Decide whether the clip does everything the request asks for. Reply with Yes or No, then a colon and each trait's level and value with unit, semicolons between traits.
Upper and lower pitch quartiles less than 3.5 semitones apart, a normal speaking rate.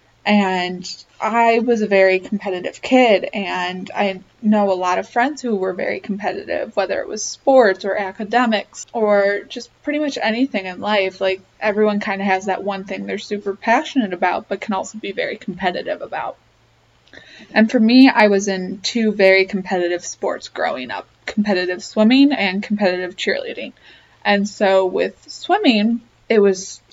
Yes: average, 3.1 semitones; average, 165 wpm